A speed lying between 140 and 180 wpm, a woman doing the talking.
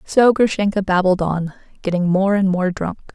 Yes: average, 170 wpm; female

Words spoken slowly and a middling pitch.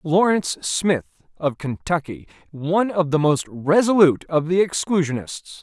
Yes: slow, 130 wpm; medium, 165 Hz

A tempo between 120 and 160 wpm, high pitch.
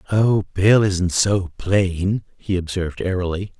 No: slow, 135 wpm; very low, 95 Hz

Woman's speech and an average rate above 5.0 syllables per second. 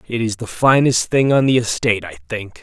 No: male; 5.6 syllables/s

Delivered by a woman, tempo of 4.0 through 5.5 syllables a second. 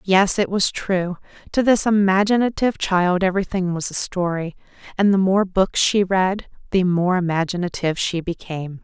Yes: female; 5.0 syllables/s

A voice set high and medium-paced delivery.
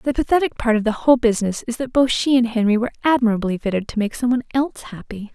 No: high, 235 Hz; fast, 245 wpm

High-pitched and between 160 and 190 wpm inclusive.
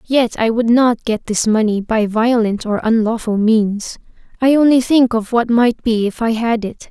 No: high, 225 Hz; average, 200 wpm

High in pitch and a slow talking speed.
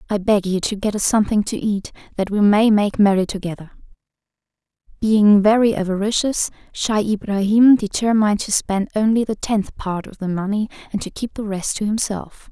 No: high, 205 Hz; average, 175 wpm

